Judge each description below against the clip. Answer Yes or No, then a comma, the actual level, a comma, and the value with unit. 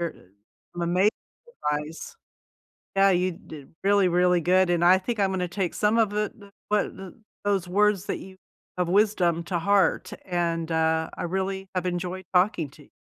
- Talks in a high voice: No, medium, 180 Hz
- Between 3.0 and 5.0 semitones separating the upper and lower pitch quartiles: No, narrow, 2.4 semitones